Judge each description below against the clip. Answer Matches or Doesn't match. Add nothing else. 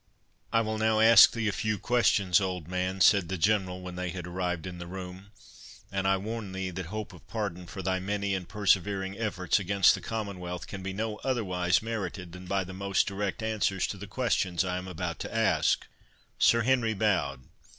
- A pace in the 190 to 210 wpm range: Matches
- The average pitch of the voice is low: Matches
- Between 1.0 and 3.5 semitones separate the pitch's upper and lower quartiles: Matches